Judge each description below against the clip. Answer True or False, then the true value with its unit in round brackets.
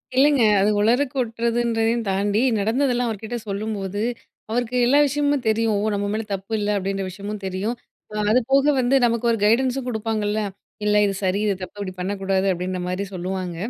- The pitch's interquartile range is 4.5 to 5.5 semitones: False (3.5 semitones)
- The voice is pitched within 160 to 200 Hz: False (215 Hz)